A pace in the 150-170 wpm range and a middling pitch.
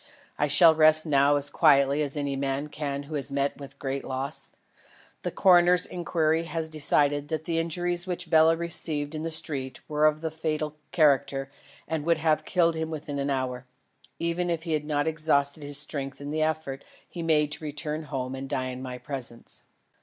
No: average, 200 wpm; medium, 150 Hz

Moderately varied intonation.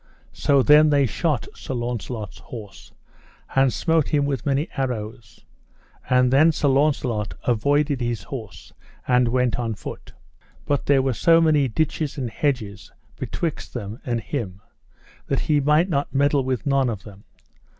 Yes: average, 3.6 semitones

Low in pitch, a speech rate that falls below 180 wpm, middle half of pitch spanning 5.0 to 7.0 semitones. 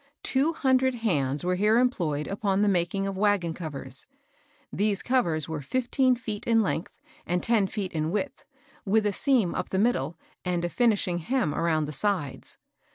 No: high, 195 Hz; average, 170 wpm; wide, 5.6 semitones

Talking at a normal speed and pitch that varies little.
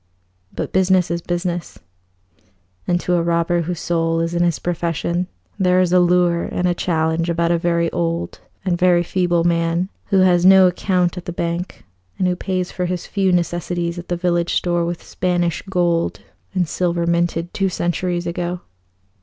Yes: average, 175 wpm; narrow, 1.0 semitones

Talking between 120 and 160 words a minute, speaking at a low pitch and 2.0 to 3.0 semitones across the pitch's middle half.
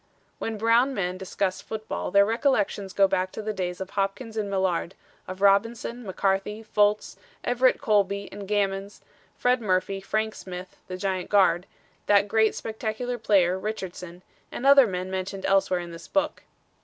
No: average, 155 wpm; high, 200 Hz; narrow, 2.6 semitones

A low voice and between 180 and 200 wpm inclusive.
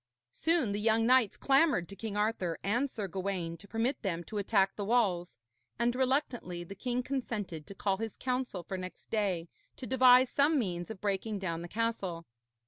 No: high, 210 Hz; average, 185 wpm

